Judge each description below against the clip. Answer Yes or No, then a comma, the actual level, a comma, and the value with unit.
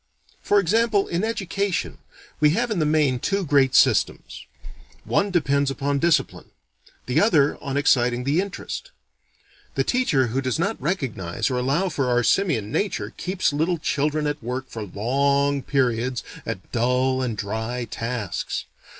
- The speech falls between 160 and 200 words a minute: No, average, 150 wpm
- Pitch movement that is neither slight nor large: No, wide, 5.8 semitones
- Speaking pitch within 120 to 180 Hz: Yes, medium, 140 Hz